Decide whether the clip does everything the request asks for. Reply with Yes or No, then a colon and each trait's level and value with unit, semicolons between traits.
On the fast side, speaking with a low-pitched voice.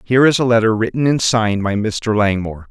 Yes: fast, 220 wpm; low, 110 Hz